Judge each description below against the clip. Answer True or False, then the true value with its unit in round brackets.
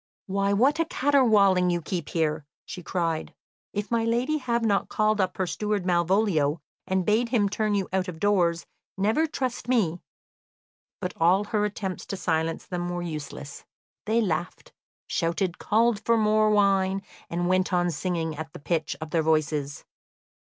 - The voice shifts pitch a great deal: False (4.1 semitones)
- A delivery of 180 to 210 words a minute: False (165 wpm)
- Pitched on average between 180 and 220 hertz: True (190 Hz)